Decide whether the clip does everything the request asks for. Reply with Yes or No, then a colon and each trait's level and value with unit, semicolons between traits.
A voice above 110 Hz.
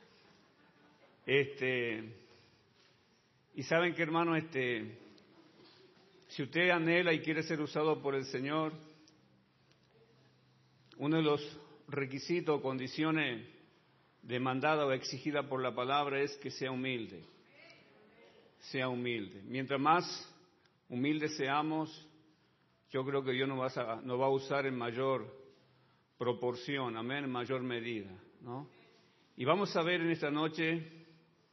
Yes: medium, 140 Hz